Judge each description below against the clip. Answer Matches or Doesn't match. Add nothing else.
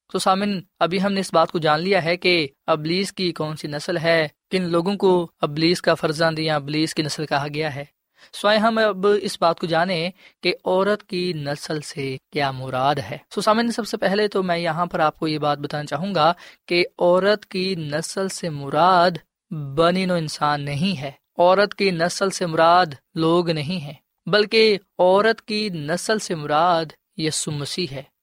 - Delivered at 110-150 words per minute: Doesn't match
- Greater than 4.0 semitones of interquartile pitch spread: Doesn't match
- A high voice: Doesn't match